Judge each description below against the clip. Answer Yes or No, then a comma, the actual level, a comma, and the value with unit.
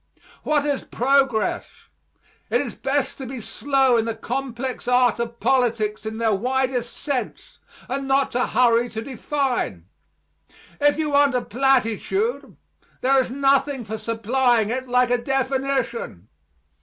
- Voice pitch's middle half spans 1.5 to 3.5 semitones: Yes, average, 2.7 semitones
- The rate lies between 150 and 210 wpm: No, average, 140 wpm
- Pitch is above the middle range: Yes, very high, 255 Hz